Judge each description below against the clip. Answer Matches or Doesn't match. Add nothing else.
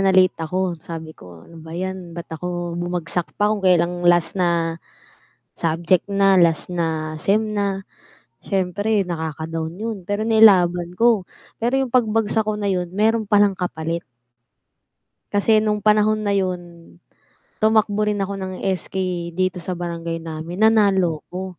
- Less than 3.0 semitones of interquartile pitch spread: Doesn't match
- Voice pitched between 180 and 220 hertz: Matches